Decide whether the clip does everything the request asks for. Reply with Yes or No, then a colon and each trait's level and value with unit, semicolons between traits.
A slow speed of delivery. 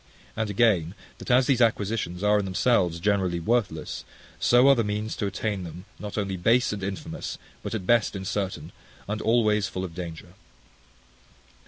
No: average, 165 wpm